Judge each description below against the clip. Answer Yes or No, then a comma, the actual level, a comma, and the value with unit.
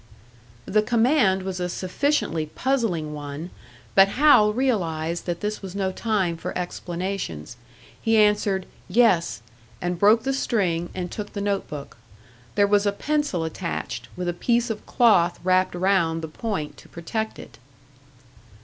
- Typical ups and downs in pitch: Yes, average, 4.2 semitones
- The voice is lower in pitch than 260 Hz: Yes, high, 190 Hz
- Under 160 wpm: Yes, average, 145 wpm